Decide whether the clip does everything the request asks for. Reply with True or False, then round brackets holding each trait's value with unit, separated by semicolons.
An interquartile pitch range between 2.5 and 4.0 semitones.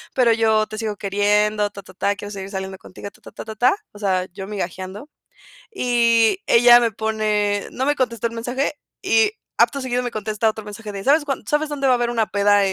True (3.0 semitones)